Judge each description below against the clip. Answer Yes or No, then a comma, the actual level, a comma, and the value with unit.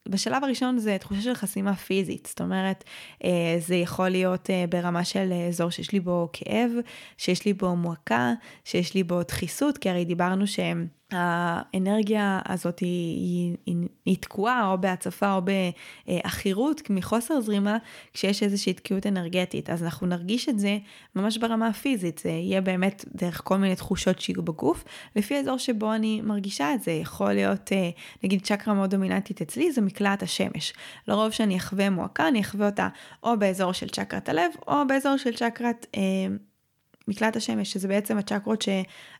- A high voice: Yes, high, 195 Hz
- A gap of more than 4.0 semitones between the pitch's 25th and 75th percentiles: No, average, 3.4 semitones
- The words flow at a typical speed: No, fast, 160 wpm